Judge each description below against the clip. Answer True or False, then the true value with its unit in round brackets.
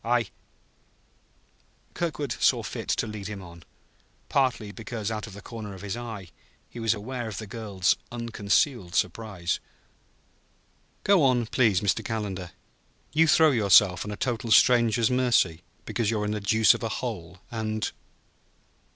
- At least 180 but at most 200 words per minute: False (155 wpm)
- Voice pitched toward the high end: False (110 Hz)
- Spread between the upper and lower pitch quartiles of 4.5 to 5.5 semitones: False (3.1 semitones)